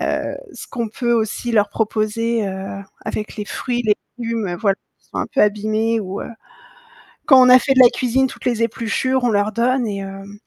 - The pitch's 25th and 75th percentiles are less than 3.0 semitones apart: Yes, narrow, 2.6 semitones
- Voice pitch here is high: Yes, high, 225 Hz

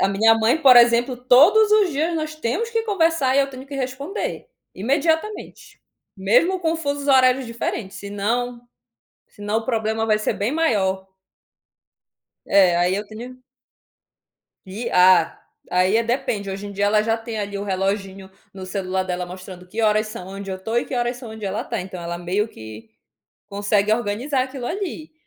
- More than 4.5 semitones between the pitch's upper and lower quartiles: Yes, average, 5.2 semitones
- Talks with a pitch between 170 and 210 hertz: No, high, 225 Hz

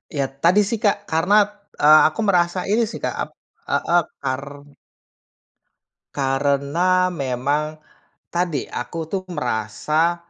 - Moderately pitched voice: Yes, medium, 160 Hz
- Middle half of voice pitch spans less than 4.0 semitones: No, average, 4.3 semitones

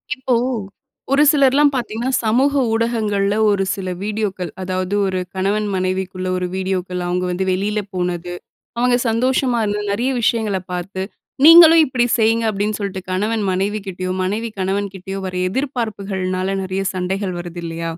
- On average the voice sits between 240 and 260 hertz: No, high, 200 Hz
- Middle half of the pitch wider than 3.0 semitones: Yes, average, 3.6 semitones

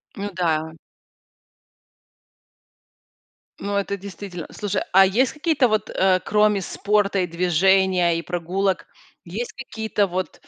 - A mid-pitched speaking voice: No, high, 195 Hz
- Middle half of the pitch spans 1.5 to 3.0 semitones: Yes, narrow, 2.6 semitones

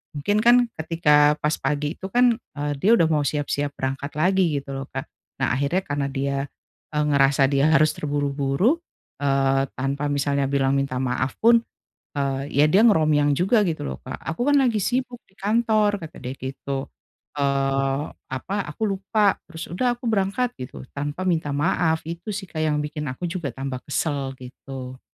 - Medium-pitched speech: Yes, medium, 150 Hz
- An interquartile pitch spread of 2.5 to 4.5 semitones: No, wide, 5.5 semitones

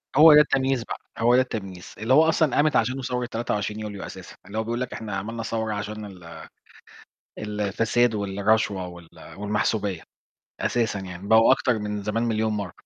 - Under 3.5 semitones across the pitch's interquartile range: Yes, average, 2.9 semitones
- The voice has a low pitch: Yes, low, 110 Hz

